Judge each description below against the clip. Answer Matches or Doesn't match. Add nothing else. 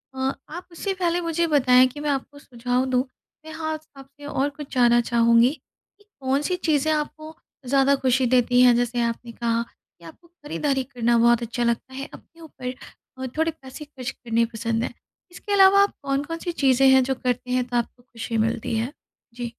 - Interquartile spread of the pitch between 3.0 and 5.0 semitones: Matches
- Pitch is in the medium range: Doesn't match